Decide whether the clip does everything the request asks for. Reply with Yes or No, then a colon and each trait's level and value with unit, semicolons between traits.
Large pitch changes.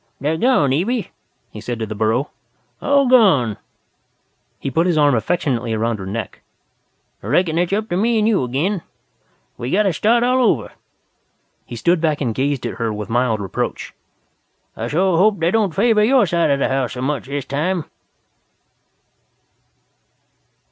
Yes: wide, 8.5 semitones